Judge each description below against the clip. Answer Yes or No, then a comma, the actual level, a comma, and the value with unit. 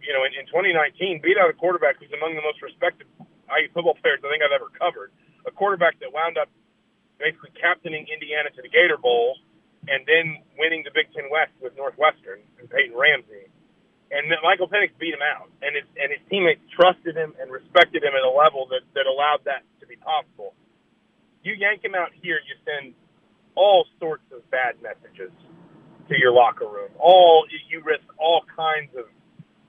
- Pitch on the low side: No, medium, 165 Hz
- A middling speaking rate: Yes, average, 190 wpm